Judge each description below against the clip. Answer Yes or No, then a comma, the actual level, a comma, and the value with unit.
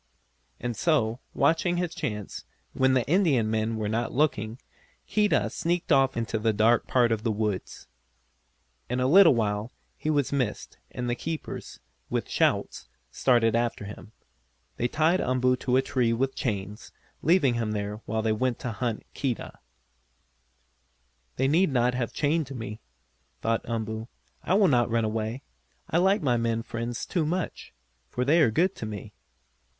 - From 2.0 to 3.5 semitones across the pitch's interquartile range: No, average, 4.4 semitones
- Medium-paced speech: Yes, average, 160 wpm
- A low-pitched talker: Yes, low, 120 Hz